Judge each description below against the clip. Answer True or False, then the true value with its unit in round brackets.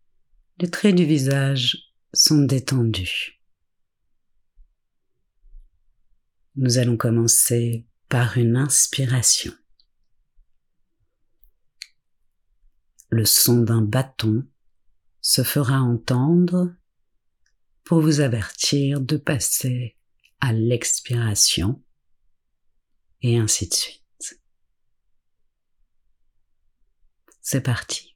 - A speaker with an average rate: False (70 wpm)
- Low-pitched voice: True (120 Hz)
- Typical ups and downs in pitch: False (7.0 semitones)